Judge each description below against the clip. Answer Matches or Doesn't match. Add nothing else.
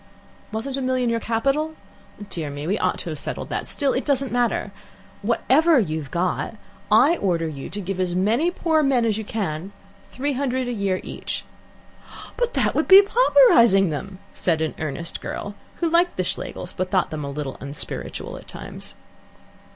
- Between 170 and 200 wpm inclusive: Matches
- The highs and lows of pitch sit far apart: Matches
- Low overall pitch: Doesn't match